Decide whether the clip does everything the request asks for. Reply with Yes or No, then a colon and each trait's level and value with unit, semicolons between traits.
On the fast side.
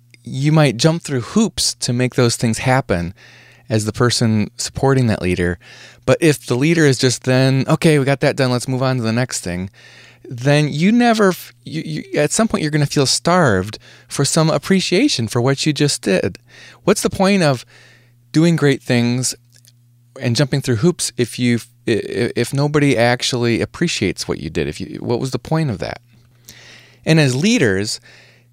No: average, 185 wpm